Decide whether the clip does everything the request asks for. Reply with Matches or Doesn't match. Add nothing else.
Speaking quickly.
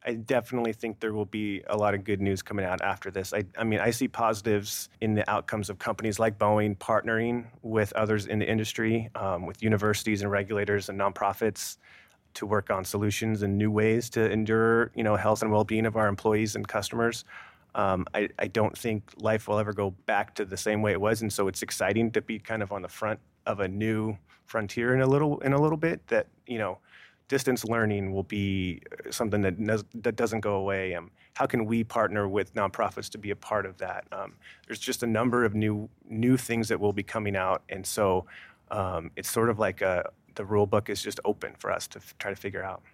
Matches